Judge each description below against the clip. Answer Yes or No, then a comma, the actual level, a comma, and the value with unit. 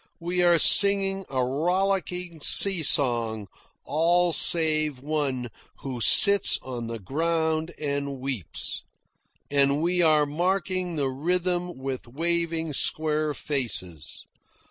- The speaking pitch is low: No, medium, 155 Hz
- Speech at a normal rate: No, slow, 110 wpm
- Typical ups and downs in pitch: Yes, average, 4.5 semitones